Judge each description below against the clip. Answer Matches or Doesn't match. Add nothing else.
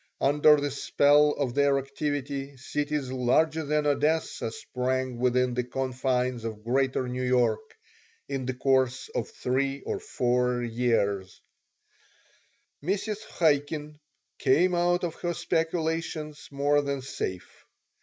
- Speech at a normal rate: Doesn't match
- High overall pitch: Doesn't match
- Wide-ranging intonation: Doesn't match